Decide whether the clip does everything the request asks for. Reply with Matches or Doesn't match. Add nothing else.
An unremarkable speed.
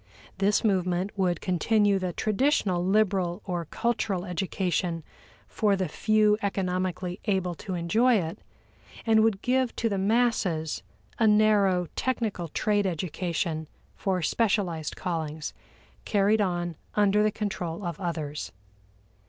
Doesn't match